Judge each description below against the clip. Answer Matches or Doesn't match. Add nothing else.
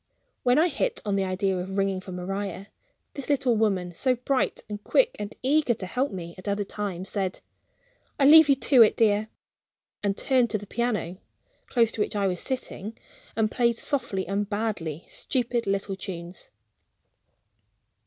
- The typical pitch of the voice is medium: Doesn't match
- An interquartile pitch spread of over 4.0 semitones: Matches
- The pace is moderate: Matches